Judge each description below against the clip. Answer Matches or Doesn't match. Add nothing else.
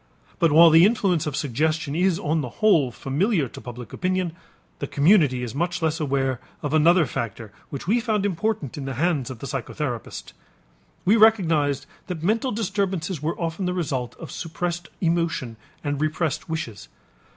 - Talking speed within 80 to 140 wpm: Doesn't match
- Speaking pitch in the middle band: Matches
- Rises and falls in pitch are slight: Doesn't match